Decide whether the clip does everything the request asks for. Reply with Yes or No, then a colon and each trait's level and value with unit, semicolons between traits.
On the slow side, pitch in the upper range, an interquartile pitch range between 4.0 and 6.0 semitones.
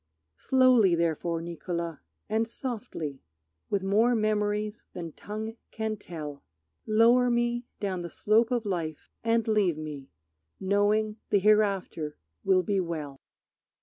Yes: slow, 120 wpm; high, 205 Hz; average, 4.6 semitones